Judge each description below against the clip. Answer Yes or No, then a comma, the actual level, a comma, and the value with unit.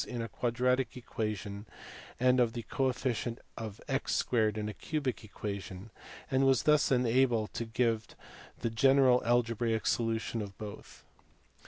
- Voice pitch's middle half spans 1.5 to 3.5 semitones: Yes, narrow, 2.5 semitones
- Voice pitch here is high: No, low, 115 Hz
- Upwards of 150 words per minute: No, average, 140 wpm